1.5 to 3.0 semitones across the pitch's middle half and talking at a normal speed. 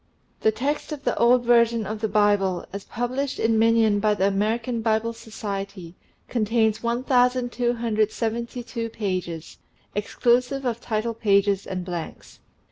No: narrow, 2.6 semitones; slow, 125 wpm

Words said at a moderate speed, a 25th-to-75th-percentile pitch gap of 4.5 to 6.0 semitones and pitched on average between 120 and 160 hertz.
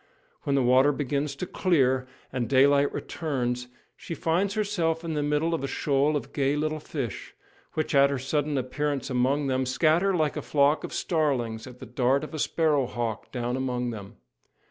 No: average, 185 wpm; average, 3.3 semitones; medium, 140 Hz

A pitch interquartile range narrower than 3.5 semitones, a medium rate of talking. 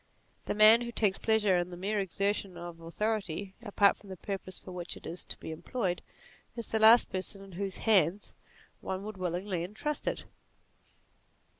Yes: average, 3.0 semitones; average, 175 wpm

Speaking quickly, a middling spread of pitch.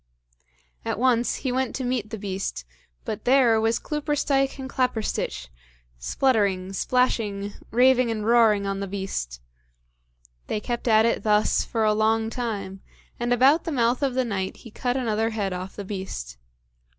No: average, 160 wpm; average, 4.0 semitones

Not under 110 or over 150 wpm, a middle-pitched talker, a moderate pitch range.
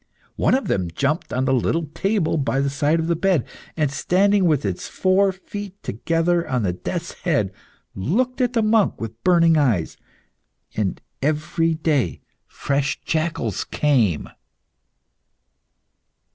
No: average, 140 wpm; medium, 155 Hz; wide, 5.7 semitones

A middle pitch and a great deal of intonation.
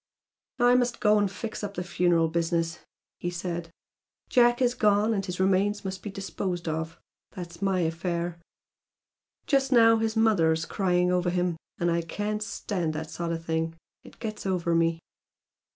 No: medium, 180 Hz; average, 3.8 semitones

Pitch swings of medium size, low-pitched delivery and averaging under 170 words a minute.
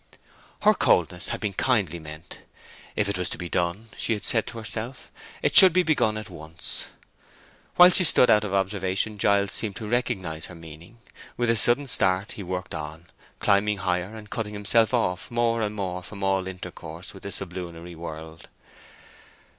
No: average, 3.8 semitones; low, 100 Hz; average, 180 wpm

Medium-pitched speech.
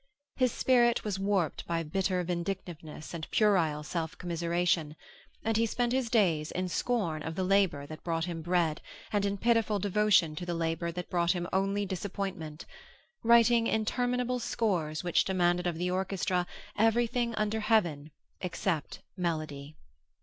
Yes: medium, 180 Hz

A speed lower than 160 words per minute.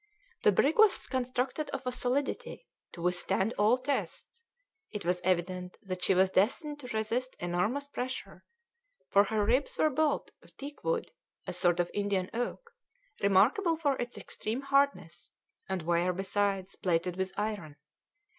Yes: average, 150 wpm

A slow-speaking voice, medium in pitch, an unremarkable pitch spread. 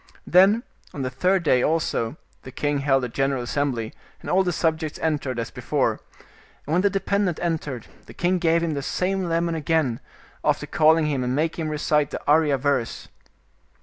No: average, 185 wpm; medium, 155 Hz; average, 3.8 semitones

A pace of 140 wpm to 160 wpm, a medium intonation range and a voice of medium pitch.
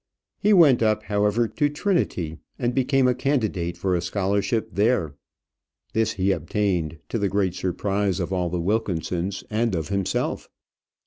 No: average, 150 wpm; average, 4.3 semitones; low, 100 Hz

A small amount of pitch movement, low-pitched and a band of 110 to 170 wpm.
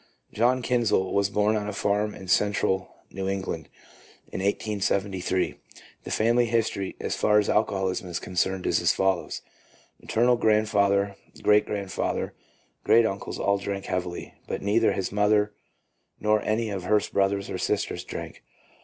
Yes: narrow, 2.0 semitones; low, 100 Hz; average, 160 wpm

